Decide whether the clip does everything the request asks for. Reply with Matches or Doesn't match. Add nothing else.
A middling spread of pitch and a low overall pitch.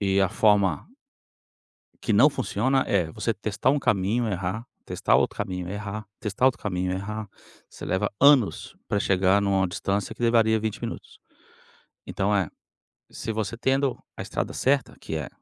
Matches